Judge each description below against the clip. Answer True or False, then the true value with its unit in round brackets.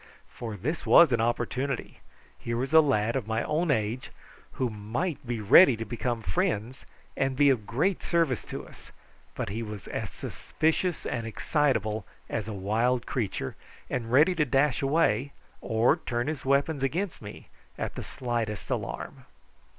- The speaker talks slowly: False (160 wpm)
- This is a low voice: True (125 Hz)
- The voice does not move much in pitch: False (4.3 semitones)